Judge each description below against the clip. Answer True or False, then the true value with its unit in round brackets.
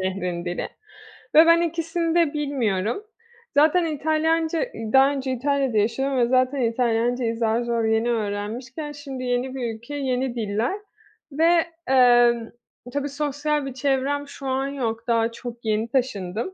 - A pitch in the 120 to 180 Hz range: False (260 Hz)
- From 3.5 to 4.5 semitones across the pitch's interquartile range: True (3.8 semitones)